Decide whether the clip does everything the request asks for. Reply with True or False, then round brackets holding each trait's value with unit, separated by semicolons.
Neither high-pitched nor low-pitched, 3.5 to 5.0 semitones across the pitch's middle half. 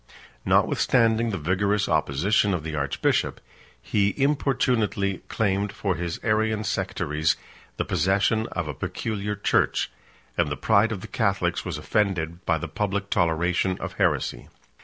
False (100 Hz; 4.2 semitones)